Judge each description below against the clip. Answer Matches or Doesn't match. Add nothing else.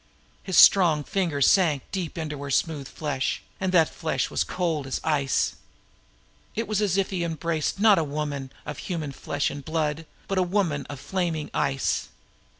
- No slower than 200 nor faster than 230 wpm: Doesn't match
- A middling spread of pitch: Matches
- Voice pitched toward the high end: Doesn't match